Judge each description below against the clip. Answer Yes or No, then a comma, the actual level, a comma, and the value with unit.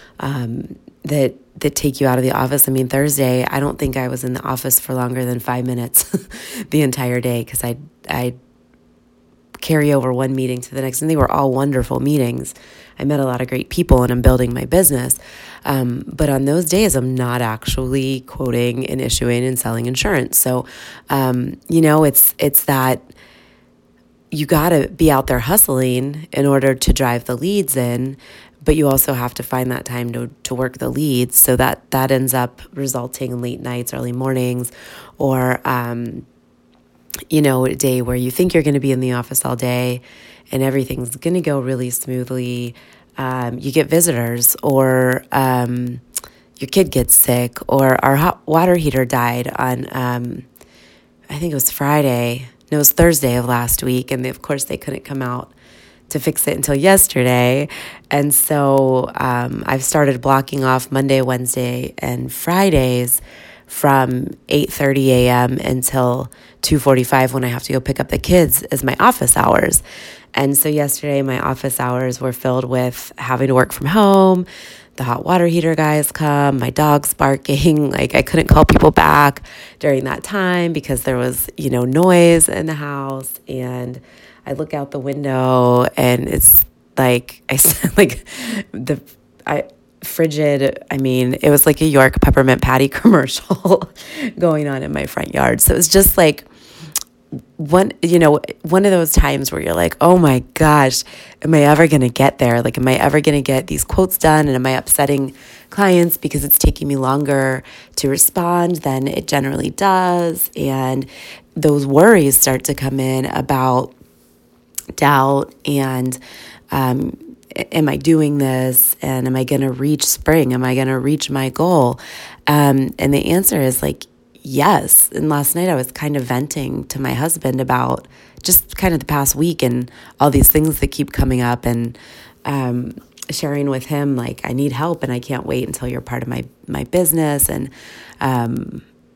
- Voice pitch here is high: No, low, 135 Hz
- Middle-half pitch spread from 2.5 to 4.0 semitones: Yes, average, 2.8 semitones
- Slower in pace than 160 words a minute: No, average, 180 wpm